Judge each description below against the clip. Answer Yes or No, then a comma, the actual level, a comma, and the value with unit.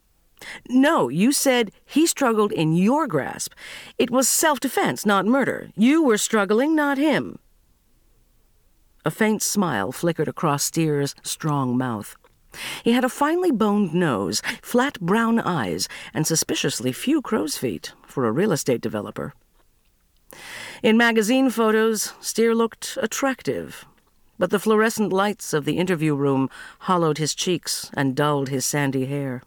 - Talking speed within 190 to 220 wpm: No, average, 140 wpm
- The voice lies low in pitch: No, high, 210 Hz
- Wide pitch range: Yes, wide, 8.3 semitones